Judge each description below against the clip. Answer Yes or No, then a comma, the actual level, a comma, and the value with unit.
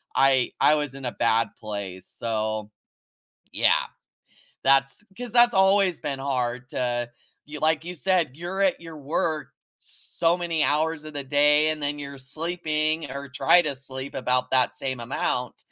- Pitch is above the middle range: No, medium, 145 Hz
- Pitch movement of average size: Yes, average, 4.0 semitones